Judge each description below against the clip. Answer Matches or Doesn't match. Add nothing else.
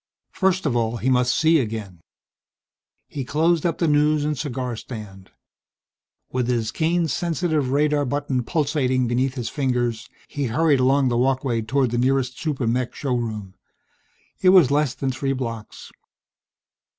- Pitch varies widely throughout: Doesn't match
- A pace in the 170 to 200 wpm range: Doesn't match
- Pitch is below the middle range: Matches